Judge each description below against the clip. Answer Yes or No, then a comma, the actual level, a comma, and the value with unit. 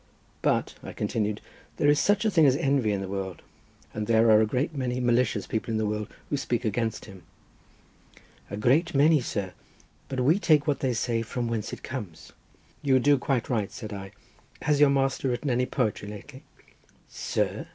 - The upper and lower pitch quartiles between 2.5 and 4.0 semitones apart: No, average, 4.6 semitones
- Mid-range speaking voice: No, low, 120 Hz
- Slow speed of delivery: No, average, 190 wpm